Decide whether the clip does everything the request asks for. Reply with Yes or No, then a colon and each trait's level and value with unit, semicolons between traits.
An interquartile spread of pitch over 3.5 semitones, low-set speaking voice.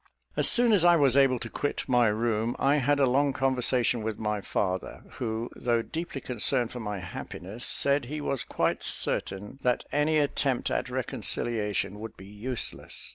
Yes: average, 4.2 semitones; low, 125 Hz